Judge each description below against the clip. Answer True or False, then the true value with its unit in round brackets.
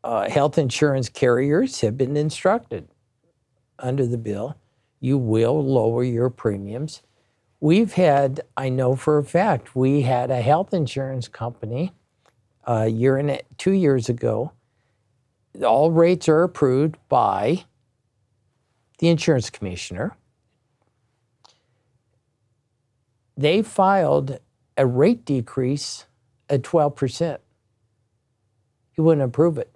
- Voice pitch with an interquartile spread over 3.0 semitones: True (3.8 semitones)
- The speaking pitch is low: True (130 Hz)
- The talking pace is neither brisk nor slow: False (110 wpm)